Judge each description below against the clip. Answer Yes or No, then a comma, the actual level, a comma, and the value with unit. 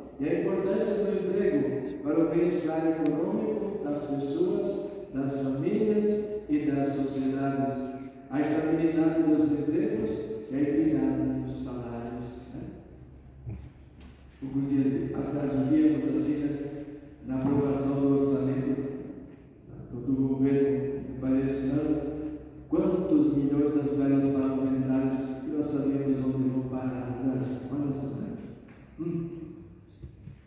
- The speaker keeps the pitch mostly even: Yes, narrow, 2.3 semitones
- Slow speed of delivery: Yes, slow, 100 wpm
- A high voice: No, medium, 140 Hz